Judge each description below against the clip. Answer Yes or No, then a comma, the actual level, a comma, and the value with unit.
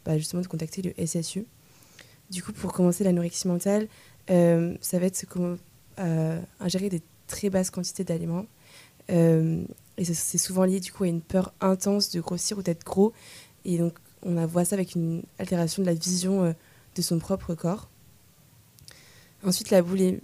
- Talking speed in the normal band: Yes, average, 180 wpm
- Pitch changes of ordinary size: No, narrow, 2.0 semitones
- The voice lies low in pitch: No, medium, 180 Hz